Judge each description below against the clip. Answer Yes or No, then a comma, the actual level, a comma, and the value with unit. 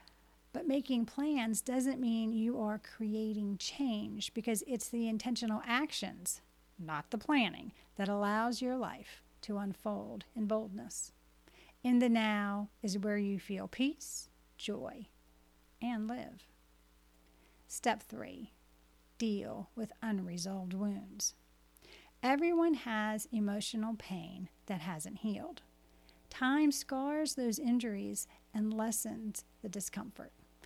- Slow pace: Yes, slow, 110 wpm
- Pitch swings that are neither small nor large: Yes, average, 4.8 semitones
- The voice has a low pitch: No, high, 215 Hz